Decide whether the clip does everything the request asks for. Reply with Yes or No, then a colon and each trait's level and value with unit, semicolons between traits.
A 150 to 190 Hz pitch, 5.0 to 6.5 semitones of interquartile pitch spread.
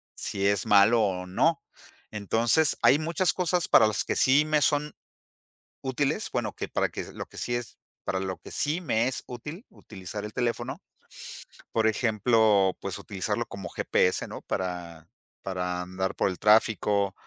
No: low, 110 Hz; wide, 5.4 semitones